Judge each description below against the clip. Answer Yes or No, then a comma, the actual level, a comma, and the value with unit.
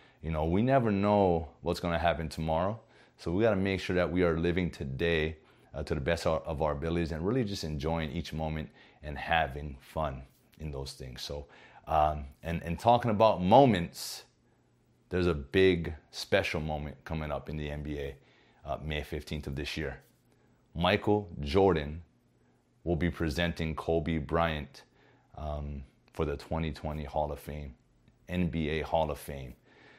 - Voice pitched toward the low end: Yes, very low, 80 Hz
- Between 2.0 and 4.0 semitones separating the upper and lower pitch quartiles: Yes, average, 2.7 semitones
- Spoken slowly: No, average, 170 wpm